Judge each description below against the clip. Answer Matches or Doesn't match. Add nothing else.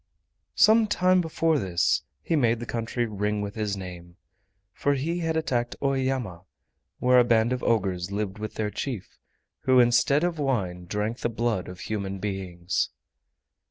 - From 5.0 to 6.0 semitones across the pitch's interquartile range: Matches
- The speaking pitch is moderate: Doesn't match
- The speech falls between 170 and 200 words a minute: Doesn't match